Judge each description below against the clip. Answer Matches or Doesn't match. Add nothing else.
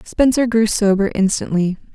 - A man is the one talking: Doesn't match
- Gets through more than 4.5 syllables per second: Matches